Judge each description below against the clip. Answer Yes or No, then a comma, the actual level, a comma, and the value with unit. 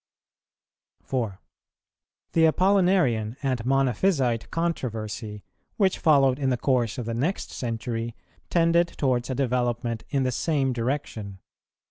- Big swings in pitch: No, average, 4.9 semitones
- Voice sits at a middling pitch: No, low, 130 Hz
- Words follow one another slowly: Yes, slow, 110 wpm